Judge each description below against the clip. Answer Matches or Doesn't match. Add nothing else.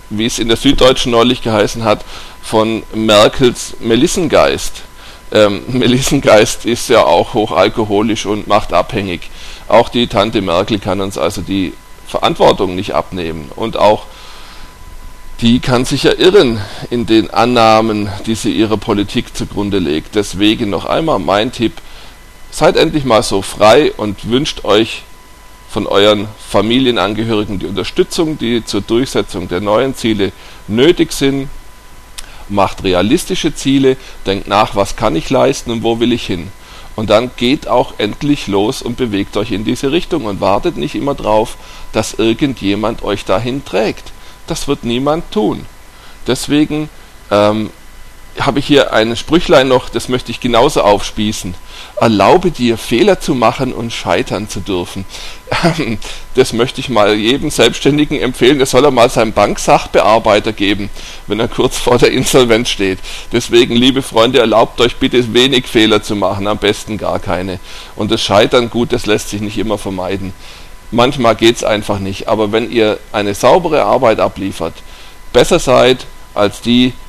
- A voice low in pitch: Matches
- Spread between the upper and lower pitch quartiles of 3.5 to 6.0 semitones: Matches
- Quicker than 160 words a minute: Doesn't match